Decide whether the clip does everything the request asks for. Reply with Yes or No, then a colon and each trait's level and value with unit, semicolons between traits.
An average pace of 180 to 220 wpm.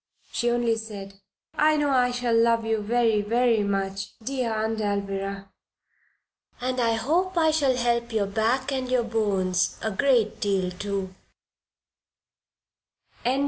No: slow, 135 wpm